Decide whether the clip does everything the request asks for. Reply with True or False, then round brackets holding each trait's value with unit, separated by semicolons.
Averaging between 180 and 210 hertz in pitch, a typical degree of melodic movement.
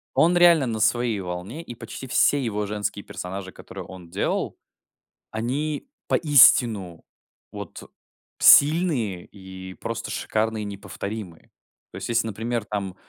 False (110 Hz; 4.2 semitones)